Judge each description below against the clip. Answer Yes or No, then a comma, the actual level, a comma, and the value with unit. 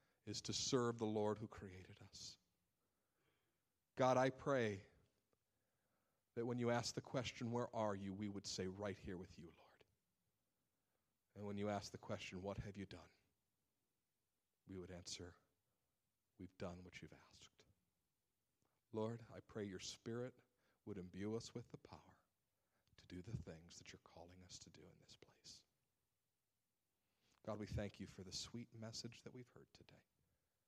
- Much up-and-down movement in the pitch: No, average, 3.9 semitones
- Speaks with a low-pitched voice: Yes, low, 105 Hz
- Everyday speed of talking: Yes, average, 160 wpm